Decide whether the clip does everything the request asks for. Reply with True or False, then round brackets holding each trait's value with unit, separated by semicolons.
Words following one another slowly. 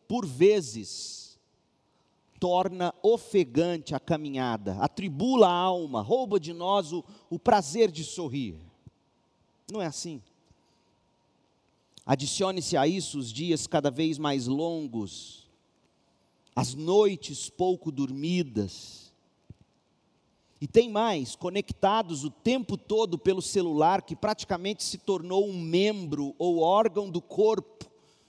True (110 wpm)